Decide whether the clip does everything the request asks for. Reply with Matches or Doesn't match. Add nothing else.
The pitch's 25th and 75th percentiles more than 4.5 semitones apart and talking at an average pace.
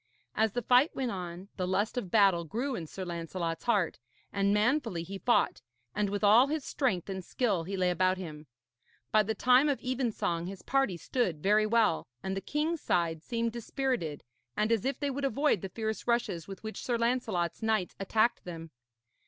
Matches